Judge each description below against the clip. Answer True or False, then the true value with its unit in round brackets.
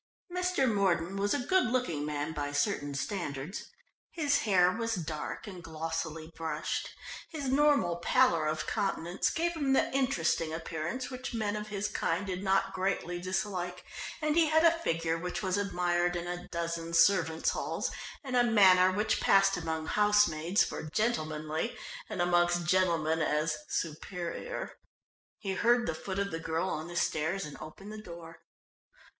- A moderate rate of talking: True (160 wpm)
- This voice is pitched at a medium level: True (180 Hz)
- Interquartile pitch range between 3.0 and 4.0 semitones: False (4.5 semitones)